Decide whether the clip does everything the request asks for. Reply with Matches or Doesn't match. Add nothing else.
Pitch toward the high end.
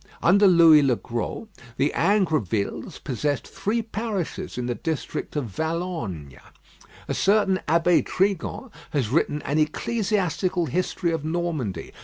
Doesn't match